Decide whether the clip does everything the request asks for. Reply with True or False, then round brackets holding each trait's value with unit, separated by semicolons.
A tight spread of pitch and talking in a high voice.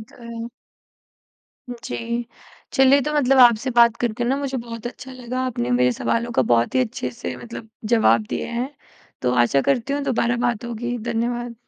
True (1.8 semitones; 240 Hz)